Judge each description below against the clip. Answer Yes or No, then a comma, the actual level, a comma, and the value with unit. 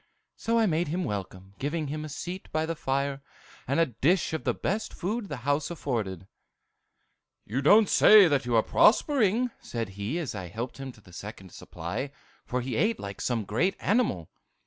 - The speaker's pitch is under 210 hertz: Yes, medium, 140 Hz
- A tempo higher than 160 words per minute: Yes, average, 185 wpm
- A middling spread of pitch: No, wide, 8.1 semitones